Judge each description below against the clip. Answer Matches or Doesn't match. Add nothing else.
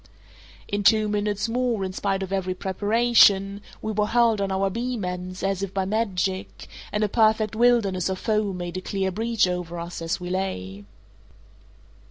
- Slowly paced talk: Doesn't match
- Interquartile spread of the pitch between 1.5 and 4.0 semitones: Matches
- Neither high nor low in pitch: Doesn't match